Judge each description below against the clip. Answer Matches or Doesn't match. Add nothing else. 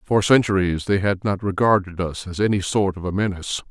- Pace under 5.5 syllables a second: Doesn't match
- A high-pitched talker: Doesn't match